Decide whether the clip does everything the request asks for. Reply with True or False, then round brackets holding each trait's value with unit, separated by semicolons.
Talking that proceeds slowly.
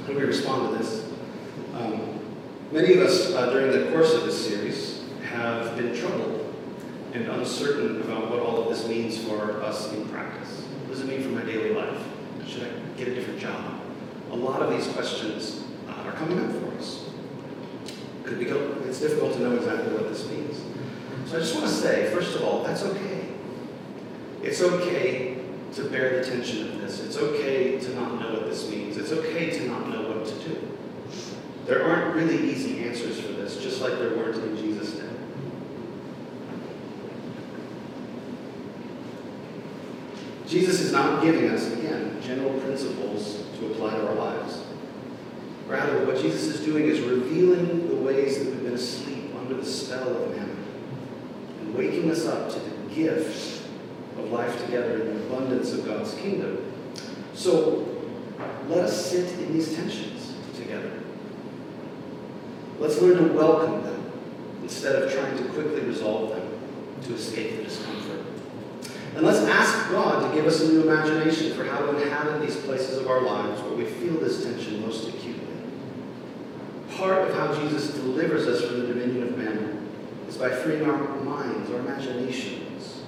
False (165 wpm)